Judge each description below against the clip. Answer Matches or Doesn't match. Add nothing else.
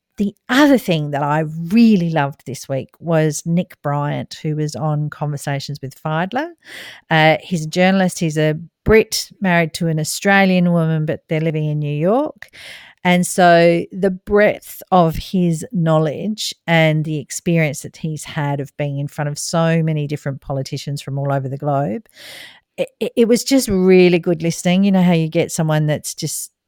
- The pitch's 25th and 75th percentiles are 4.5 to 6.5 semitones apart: Doesn't match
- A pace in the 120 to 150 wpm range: Doesn't match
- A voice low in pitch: Doesn't match